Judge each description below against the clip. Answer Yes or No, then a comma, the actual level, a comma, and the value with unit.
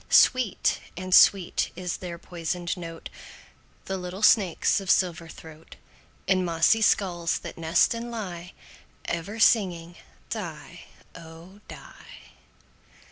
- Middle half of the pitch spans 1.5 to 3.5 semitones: Yes, average, 2.7 semitones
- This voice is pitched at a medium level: Yes, medium, 180 Hz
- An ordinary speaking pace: No, slow, 115 wpm